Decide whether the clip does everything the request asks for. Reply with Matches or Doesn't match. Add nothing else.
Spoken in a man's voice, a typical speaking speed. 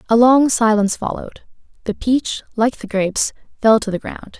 Doesn't match